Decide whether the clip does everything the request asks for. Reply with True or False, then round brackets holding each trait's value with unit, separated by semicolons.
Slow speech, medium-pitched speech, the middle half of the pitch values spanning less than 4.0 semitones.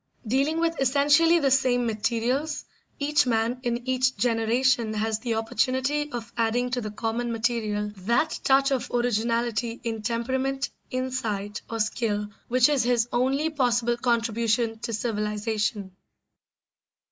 False (130 wpm; 240 Hz; 2.6 semitones)